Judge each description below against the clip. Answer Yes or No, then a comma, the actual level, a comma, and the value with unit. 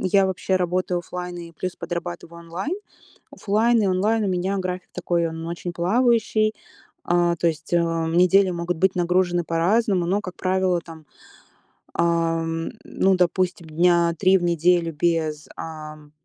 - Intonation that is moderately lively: No, narrow, 2.0 semitones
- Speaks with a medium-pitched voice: Yes, medium, 175 Hz